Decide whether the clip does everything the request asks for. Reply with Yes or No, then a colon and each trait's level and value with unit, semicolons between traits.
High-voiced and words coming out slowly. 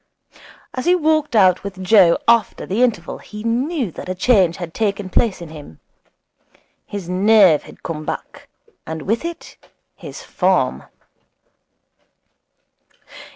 Yes: high, 200 Hz; slow, 130 wpm